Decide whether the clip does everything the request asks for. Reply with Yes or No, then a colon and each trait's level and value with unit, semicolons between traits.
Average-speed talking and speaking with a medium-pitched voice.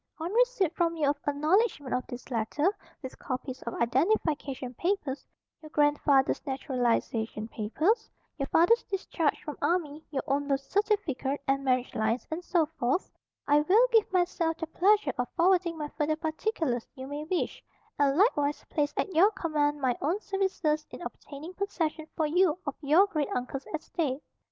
No: average, 160 wpm; very high, 305 Hz